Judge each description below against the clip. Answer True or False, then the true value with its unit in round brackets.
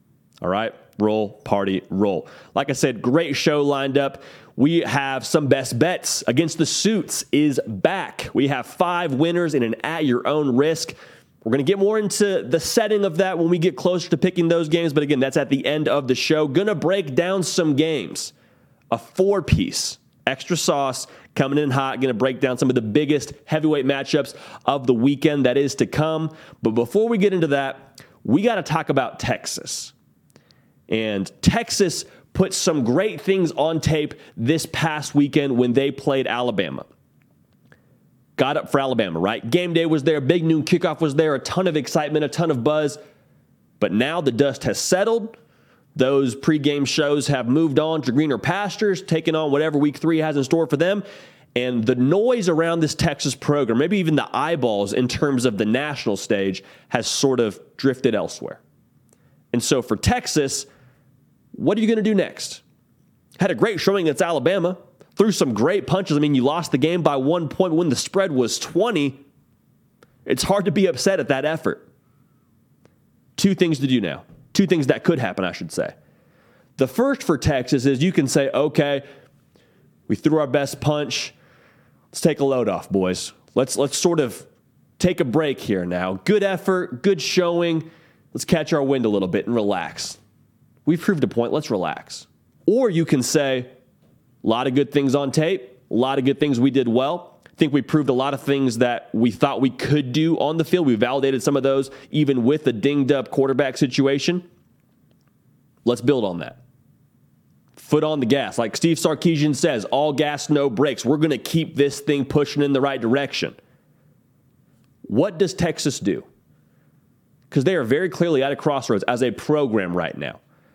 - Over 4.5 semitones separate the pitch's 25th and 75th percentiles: False (3.7 semitones)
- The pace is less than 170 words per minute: False (190 wpm)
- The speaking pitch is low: False (145 Hz)